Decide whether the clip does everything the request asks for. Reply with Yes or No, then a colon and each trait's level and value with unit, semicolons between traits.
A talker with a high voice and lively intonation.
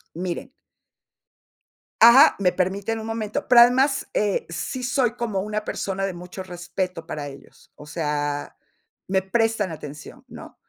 No: high, 195 Hz; average, 4.6 semitones